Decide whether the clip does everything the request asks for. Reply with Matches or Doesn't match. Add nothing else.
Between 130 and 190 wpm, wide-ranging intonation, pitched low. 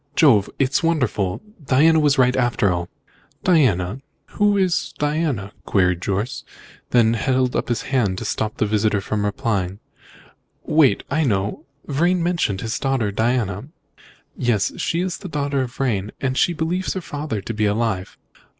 Matches